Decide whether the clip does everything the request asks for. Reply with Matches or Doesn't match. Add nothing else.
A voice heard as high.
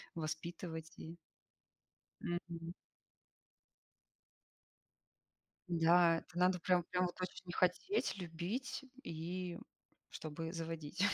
Doesn't match